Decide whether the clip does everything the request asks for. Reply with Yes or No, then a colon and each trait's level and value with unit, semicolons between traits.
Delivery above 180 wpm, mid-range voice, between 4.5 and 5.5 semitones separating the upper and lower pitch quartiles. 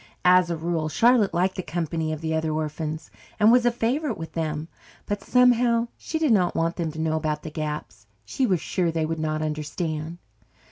Yes: average, 200 wpm; medium, 165 Hz; average, 4.8 semitones